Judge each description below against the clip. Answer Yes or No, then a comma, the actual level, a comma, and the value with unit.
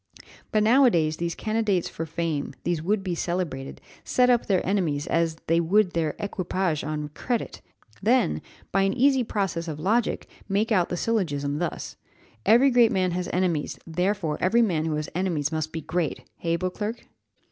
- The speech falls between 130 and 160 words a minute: No, average, 175 wpm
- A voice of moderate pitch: Yes, medium, 180 Hz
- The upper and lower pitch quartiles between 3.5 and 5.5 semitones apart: Yes, average, 4.7 semitones